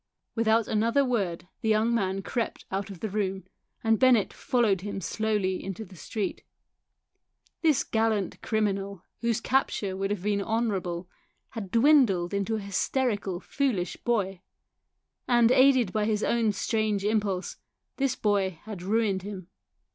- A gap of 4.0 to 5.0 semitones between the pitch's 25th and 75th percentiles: No, average, 3.0 semitones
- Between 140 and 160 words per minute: Yes, average, 145 wpm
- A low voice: No, high, 210 Hz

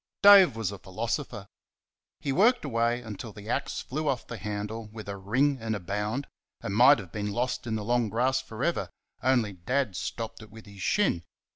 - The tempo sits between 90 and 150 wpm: No, average, 195 wpm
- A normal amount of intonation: Yes, average, 4.1 semitones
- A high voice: No, low, 115 Hz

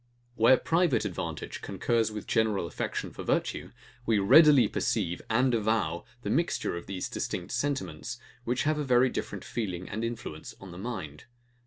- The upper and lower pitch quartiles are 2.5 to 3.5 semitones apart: No, average, 4.6 semitones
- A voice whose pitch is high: No, low, 115 Hz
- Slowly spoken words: No, average, 160 wpm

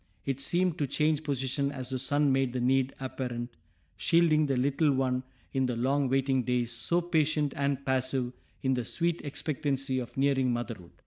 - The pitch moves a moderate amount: No, narrow, 2.2 semitones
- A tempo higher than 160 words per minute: Yes, average, 175 wpm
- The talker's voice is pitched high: No, low, 135 Hz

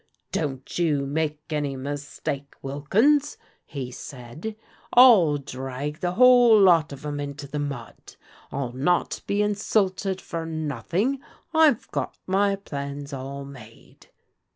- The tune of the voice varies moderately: No, wide, 5.8 semitones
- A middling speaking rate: No, slow, 130 wpm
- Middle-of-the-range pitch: Yes, medium, 150 Hz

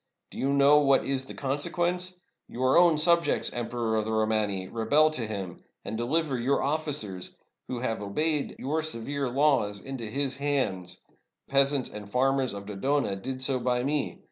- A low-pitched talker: Yes, low, 130 Hz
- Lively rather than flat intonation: No, average, 4.6 semitones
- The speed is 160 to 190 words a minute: Yes, average, 180 wpm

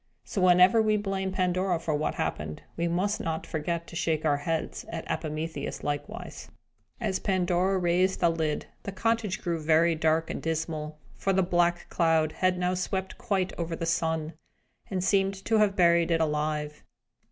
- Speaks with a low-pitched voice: No, medium, 170 Hz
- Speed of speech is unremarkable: Yes, average, 170 wpm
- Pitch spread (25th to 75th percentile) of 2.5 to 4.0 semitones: Yes, average, 2.9 semitones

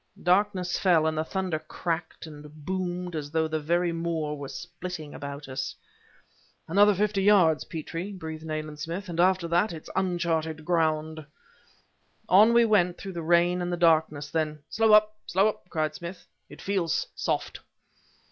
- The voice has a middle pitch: Yes, medium, 170 Hz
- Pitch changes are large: No, average, 2.9 semitones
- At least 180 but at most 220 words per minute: No, average, 160 wpm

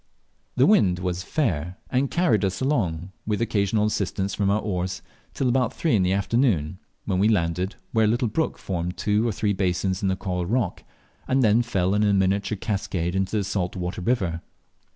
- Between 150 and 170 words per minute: No, average, 195 wpm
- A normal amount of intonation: Yes, average, 3.5 semitones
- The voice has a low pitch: Yes, low, 100 Hz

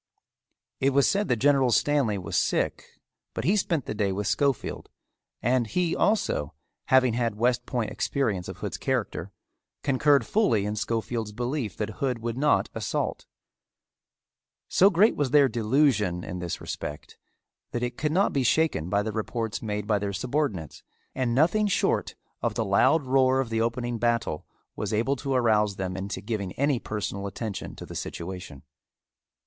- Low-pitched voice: Yes, low, 120 Hz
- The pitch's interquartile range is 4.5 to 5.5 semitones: Yes, average, 4.9 semitones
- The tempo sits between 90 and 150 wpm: No, average, 165 wpm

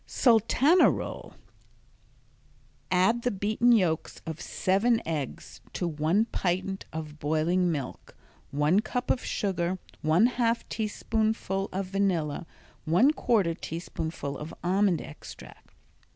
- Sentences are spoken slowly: Yes, slow, 110 wpm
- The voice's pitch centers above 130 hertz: Yes, medium, 185 Hz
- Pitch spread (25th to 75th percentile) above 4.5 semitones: Yes, average, 5.3 semitones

